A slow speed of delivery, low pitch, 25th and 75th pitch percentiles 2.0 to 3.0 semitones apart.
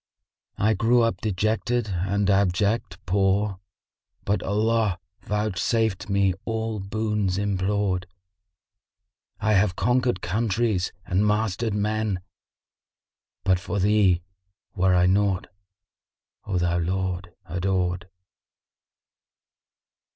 Yes: slow, 100 wpm; low, 100 Hz; narrow, 2.6 semitones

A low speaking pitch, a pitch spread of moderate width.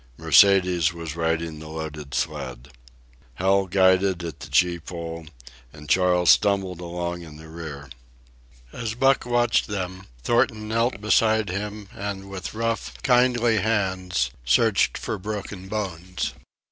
Yes: very low, 95 Hz; average, 4.2 semitones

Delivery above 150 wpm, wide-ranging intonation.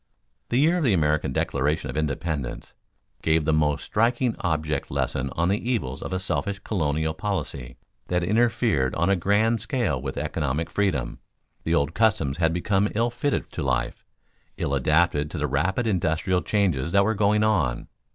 Yes: average, 170 wpm; wide, 6.3 semitones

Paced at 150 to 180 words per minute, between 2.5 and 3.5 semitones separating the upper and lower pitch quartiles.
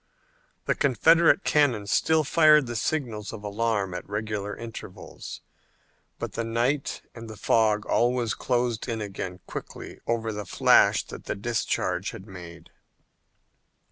No: slow, 135 wpm; average, 3.1 semitones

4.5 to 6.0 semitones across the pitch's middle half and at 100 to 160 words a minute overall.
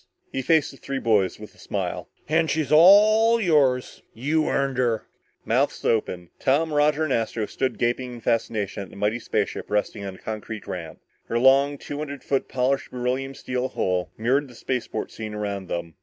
No: average, 4.9 semitones; average, 185 wpm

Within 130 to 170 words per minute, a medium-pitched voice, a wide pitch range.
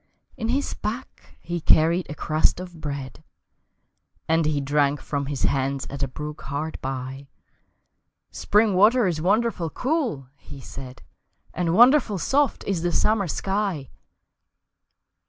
Yes: slow, 135 wpm; medium, 165 Hz; wide, 6.7 semitones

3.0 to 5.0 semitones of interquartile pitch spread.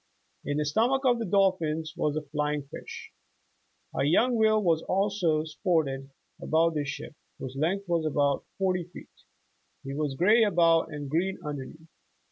Yes: average, 4.6 semitones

